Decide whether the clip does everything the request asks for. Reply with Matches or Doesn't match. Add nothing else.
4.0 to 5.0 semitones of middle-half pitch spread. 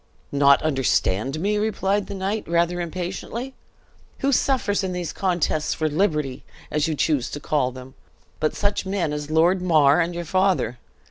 Matches